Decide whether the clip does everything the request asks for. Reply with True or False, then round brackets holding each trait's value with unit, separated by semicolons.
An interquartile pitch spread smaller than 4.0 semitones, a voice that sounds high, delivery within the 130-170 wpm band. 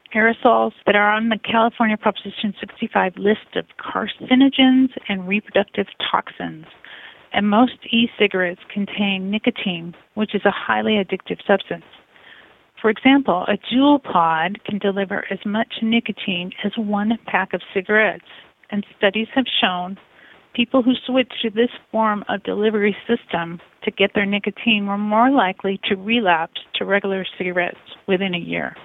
True (2.8 semitones; 210 Hz; 140 wpm)